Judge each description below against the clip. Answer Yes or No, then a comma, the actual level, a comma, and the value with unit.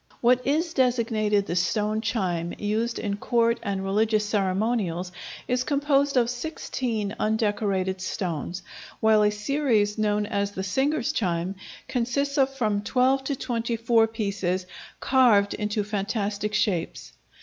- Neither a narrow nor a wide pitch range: Yes, average, 3.5 semitones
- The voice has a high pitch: Yes, high, 215 Hz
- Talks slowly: Yes, slow, 125 wpm